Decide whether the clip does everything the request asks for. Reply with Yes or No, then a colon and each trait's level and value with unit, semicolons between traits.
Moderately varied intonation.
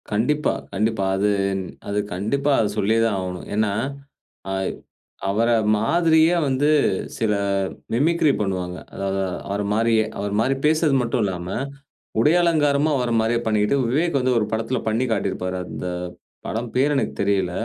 No: wide, 5.7 semitones